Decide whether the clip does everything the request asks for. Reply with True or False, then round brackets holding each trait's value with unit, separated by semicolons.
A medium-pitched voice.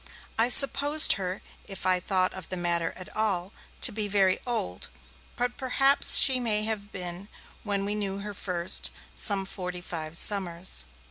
False (195 Hz)